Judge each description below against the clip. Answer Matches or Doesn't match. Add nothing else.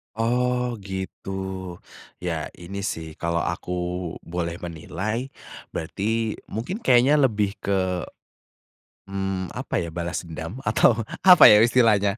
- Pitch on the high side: Doesn't match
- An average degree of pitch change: Matches